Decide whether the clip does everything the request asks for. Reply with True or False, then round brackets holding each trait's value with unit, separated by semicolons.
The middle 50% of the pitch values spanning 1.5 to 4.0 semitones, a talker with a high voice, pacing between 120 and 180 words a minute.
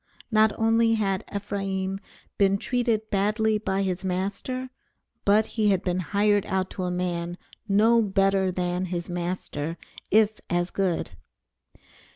True (2.8 semitones; 195 Hz; 135 wpm)